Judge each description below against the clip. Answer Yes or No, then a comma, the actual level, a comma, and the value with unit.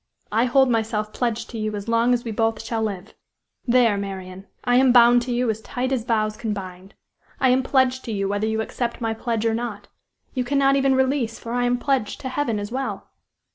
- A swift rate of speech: Yes, fast, 220 wpm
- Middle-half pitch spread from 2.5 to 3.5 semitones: Yes, average, 2.8 semitones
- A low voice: No, high, 235 Hz